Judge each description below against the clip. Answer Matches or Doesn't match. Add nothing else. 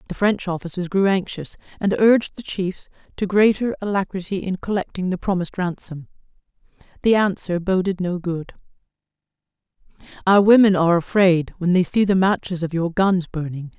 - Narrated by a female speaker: Matches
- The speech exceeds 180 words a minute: Doesn't match